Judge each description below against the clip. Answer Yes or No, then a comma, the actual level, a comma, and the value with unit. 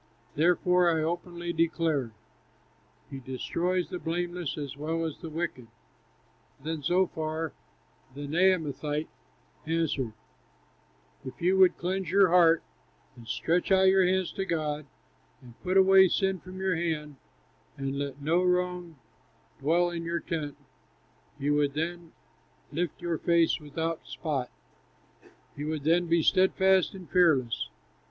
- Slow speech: Yes, slow, 130 wpm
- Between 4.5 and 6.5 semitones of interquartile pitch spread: No, average, 3.1 semitones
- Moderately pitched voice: Yes, medium, 165 Hz